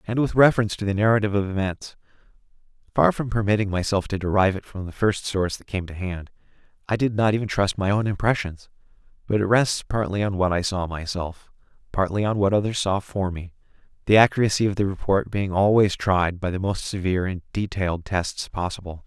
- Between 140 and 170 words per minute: No, average, 200 wpm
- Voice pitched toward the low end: Yes, low, 100 Hz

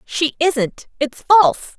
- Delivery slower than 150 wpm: Yes, slow, 135 wpm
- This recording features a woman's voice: Yes, female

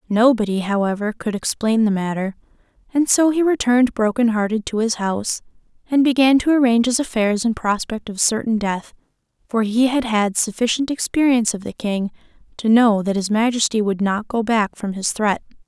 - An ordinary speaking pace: Yes, average, 180 wpm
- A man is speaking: No, female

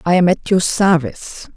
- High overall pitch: No, medium, 170 Hz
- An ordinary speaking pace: Yes, average, 190 wpm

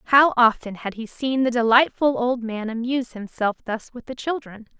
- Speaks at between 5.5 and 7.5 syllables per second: No, 5.1 syllables/s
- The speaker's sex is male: No, female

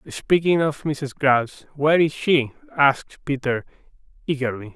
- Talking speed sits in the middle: No, slow, 125 wpm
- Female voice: No, male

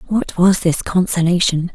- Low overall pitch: No, medium, 180 Hz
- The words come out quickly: No, slow, 135 wpm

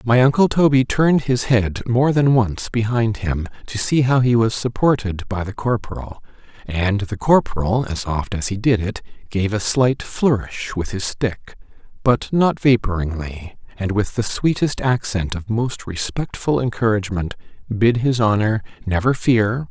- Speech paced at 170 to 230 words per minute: No, average, 160 wpm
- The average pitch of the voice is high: No, low, 115 Hz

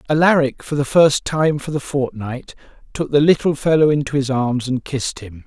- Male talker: Yes, male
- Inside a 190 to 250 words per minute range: Yes, average, 200 wpm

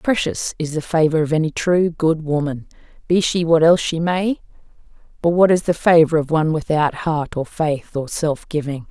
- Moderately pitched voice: Yes, medium, 160 Hz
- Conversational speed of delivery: Yes, average, 195 wpm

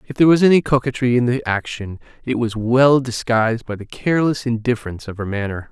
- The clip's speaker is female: No, male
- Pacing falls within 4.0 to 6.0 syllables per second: No, 6.2 syllables/s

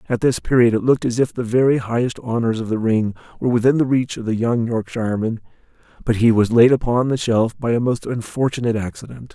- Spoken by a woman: No, male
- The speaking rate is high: Yes, fast, 220 wpm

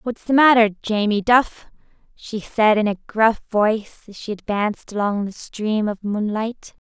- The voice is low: No, high, 215 Hz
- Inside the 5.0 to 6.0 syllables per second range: No, 4.4 syllables/s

